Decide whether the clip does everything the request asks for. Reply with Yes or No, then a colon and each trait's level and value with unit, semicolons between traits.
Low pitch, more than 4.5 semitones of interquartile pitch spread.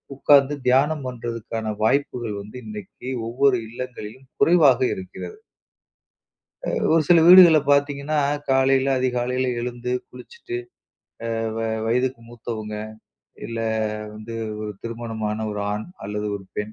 No: low, 125 Hz; average, 4.0 semitones